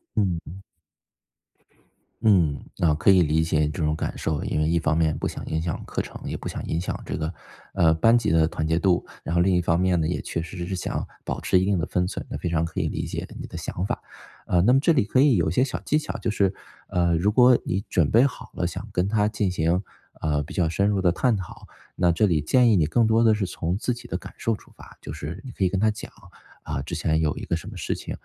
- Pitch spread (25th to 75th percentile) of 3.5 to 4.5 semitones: Yes, average, 4.2 semitones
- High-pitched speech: No, very low, 90 Hz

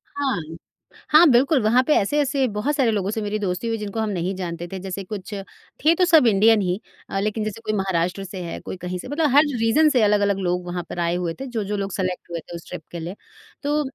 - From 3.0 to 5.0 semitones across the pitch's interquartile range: No, wide, 5.4 semitones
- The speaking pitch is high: Yes, high, 205 Hz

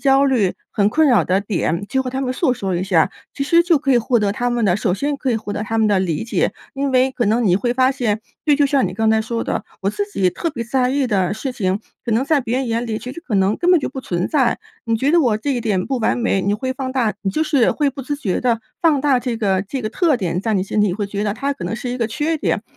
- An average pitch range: Yes, average, 4.6 semitones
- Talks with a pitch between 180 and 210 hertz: No, high, 240 Hz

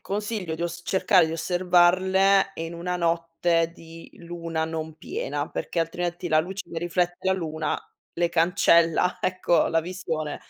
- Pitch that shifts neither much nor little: No, narrow, 1.7 semitones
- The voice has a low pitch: No, medium, 175 Hz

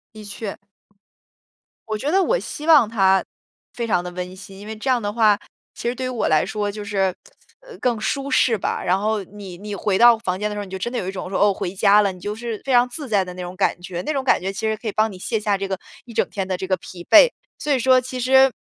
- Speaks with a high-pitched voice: Yes, high, 210 Hz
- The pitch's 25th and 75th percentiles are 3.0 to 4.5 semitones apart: Yes, average, 4.0 semitones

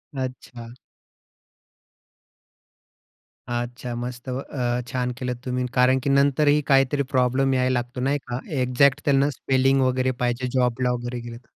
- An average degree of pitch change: No, narrow, 1.5 semitones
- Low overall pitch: Yes, low, 125 Hz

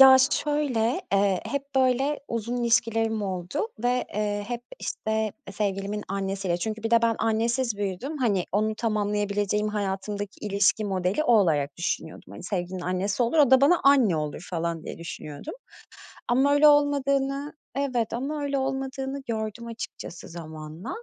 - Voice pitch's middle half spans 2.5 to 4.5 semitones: No, average, 5.2 semitones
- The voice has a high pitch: Yes, high, 220 Hz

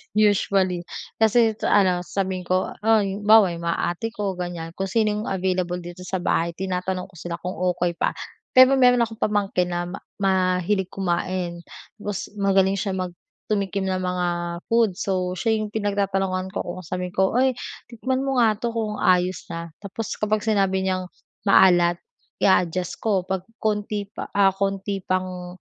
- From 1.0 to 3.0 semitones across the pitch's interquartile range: Yes, narrow, 2.4 semitones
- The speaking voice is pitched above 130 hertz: Yes, high, 190 Hz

